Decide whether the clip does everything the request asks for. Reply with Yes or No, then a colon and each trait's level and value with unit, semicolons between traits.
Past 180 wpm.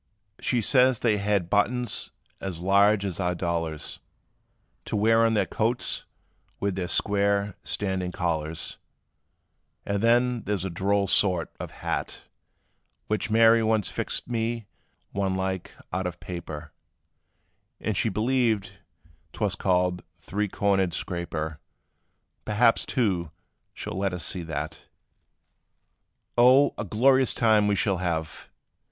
No: slow, 135 wpm